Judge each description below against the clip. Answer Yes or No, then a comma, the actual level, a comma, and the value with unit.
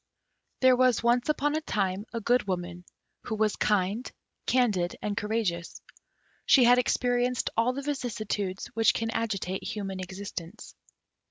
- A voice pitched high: Yes, high, 220 Hz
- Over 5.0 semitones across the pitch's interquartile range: No, average, 4.4 semitones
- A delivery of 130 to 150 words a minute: Yes, average, 140 wpm